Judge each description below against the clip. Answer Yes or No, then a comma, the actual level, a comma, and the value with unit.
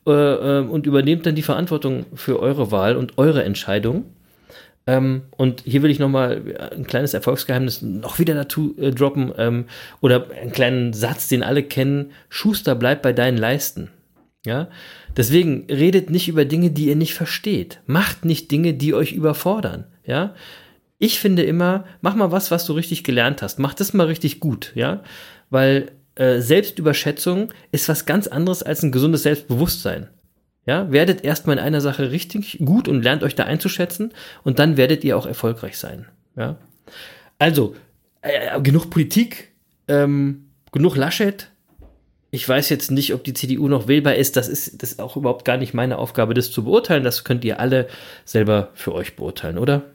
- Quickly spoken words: No, average, 170 wpm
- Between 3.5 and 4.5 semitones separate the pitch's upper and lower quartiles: Yes, average, 4.0 semitones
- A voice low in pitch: No, medium, 145 Hz